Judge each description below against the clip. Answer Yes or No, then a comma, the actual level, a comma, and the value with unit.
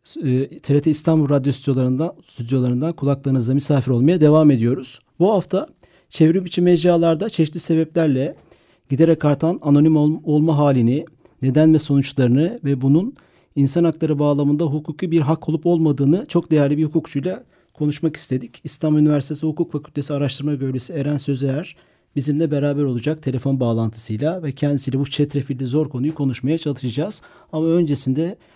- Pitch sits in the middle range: Yes, medium, 150 Hz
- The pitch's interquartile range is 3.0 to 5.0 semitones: No, narrow, 2.6 semitones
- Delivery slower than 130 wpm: No, average, 135 wpm